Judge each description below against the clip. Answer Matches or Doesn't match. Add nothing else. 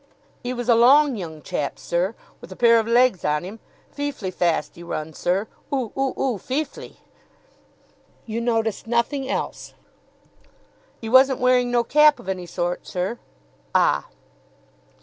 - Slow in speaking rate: Doesn't match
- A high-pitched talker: Matches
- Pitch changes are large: Matches